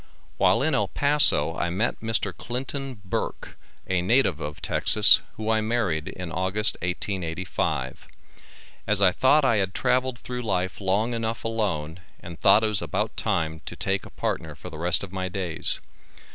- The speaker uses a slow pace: No, average, 170 wpm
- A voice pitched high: No, low, 100 Hz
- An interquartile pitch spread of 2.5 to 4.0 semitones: No, average, 4.4 semitones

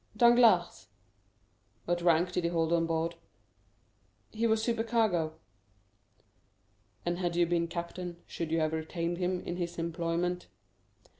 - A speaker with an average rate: No, slow, 130 wpm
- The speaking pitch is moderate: Yes, medium, 175 Hz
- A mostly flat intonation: Yes, narrow, 1.4 semitones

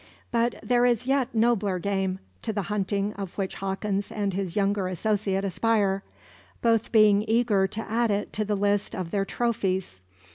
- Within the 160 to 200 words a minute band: Yes, average, 175 wpm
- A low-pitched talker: No, high, 205 Hz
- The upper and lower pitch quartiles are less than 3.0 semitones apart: Yes, narrow, 2.4 semitones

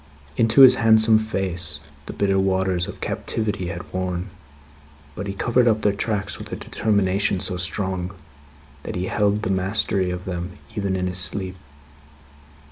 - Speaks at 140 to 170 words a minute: Yes, average, 155 wpm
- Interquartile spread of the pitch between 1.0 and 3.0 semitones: Yes, narrow, 2.4 semitones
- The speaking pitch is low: Yes, very low, 95 Hz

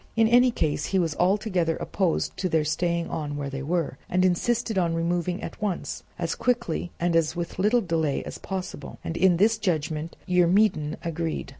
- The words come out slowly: No, average, 180 wpm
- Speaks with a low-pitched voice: No, medium, 175 Hz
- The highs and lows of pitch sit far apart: No, average, 3.0 semitones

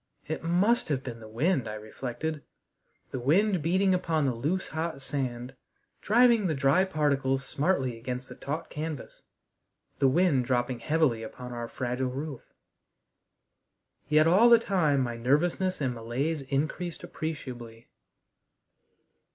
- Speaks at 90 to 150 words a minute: Yes, slow, 135 wpm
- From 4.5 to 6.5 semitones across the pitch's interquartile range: Yes, average, 4.9 semitones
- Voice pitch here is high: No, medium, 140 Hz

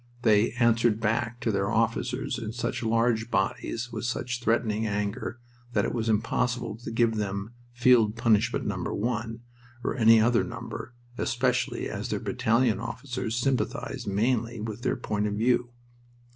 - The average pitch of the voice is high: No, low, 115 Hz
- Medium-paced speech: Yes, average, 150 wpm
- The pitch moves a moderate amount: No, narrow, 1.8 semitones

